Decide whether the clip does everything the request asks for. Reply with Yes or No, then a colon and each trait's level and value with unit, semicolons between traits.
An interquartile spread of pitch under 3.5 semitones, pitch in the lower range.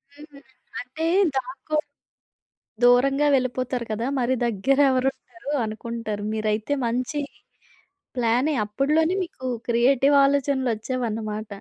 No: average, 3.1 semitones; very high, 255 Hz